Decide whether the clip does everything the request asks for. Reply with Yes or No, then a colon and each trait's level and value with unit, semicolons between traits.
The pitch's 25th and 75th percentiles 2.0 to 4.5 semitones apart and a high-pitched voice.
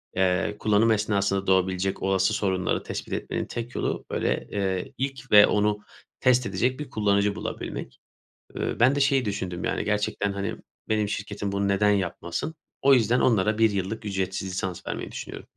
No: narrow, 2.6 semitones; low, 100 Hz